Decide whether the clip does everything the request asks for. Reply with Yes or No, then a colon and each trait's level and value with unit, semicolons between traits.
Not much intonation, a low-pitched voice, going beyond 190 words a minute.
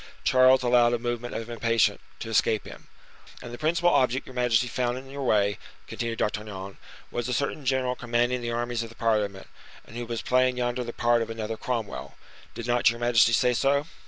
Yes: narrow, 1.7 semitones; low, 120 Hz; average, 200 wpm